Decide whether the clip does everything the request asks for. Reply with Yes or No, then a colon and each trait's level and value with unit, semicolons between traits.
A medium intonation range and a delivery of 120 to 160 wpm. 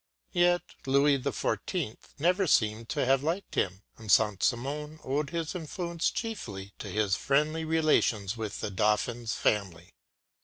No: wide, 7.1 semitones; average, 145 wpm